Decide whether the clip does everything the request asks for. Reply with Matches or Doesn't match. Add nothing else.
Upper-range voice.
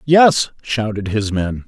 Doesn't match